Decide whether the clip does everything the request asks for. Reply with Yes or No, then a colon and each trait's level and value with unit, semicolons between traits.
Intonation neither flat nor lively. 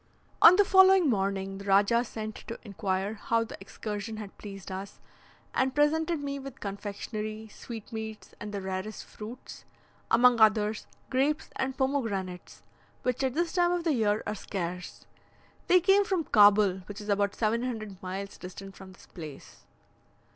Yes: average, 4.9 semitones